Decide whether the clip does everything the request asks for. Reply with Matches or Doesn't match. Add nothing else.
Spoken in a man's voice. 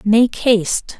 Doesn't match